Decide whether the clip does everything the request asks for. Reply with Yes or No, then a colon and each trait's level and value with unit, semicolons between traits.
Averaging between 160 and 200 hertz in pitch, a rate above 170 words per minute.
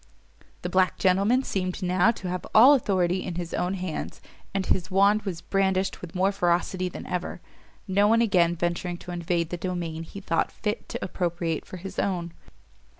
Yes: medium, 185 Hz; average, 180 wpm